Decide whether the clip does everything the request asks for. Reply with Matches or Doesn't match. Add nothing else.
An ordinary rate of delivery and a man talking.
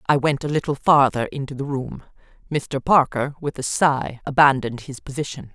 Doesn't match